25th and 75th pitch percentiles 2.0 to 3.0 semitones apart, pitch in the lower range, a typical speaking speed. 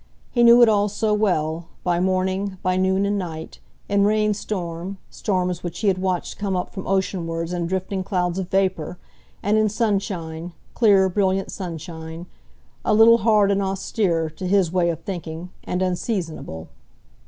No: narrow, 2.6 semitones; high, 190 Hz; average, 160 wpm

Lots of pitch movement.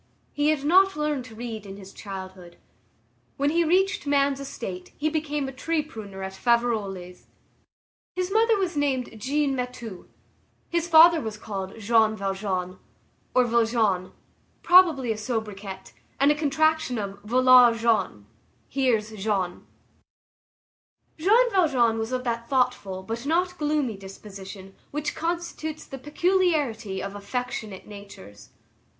Yes: wide, 7.0 semitones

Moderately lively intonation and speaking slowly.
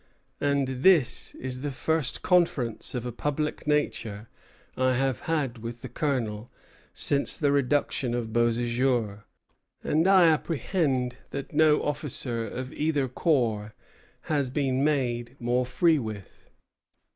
Yes: average, 3.7 semitones; slow, 125 wpm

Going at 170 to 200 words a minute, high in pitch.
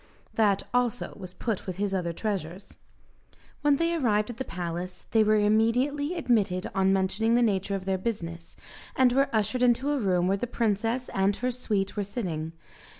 Yes: average, 180 wpm; high, 210 Hz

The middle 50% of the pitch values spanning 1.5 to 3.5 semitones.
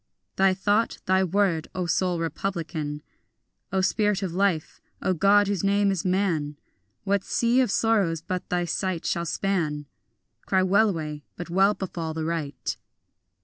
Yes: average, 3.2 semitones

